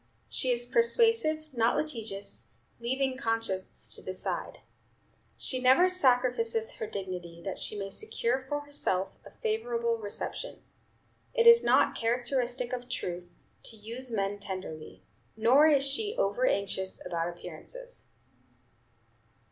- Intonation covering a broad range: Yes, wide, 7.2 semitones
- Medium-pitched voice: No, high, 245 Hz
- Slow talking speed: Yes, slow, 125 wpm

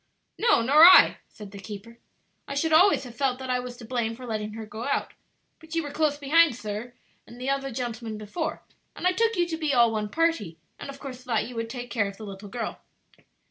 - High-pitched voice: Yes, very high, 250 Hz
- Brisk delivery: Yes, fast, 235 wpm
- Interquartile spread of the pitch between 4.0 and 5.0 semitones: Yes, average, 4.7 semitones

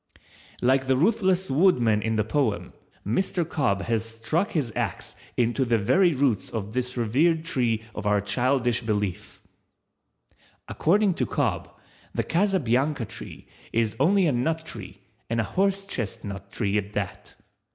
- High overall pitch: No, low, 125 Hz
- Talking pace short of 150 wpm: Yes, average, 140 wpm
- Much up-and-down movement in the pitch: Yes, wide, 6.9 semitones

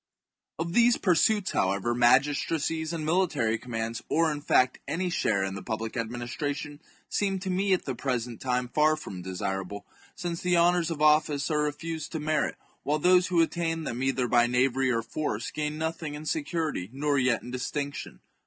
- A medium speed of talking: Yes, average, 185 wpm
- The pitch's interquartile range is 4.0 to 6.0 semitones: Yes, average, 5.2 semitones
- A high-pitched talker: No, medium, 150 Hz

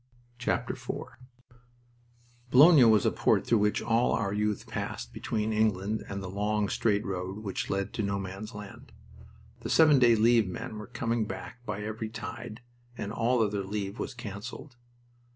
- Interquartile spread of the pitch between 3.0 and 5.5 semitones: No, narrow, 2.5 semitones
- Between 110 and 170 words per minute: Yes, average, 160 wpm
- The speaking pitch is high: No, low, 105 Hz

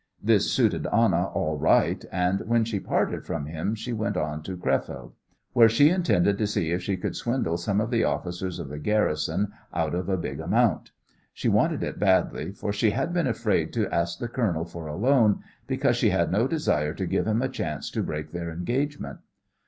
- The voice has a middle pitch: No, very low, 95 Hz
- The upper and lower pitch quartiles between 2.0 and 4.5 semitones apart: No, wide, 5.4 semitones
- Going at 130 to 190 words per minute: No, fast, 205 wpm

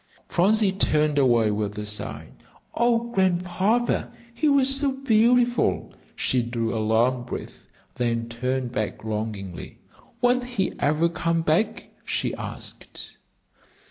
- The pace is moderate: No, slow, 120 wpm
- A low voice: No, medium, 155 Hz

